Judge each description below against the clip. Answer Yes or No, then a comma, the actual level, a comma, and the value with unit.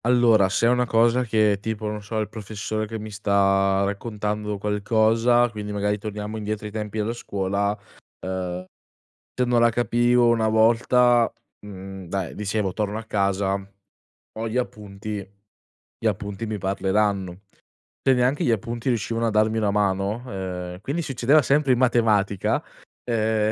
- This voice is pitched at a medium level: No, low, 105 Hz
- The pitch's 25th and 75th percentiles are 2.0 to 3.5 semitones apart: Yes, narrow, 2.6 semitones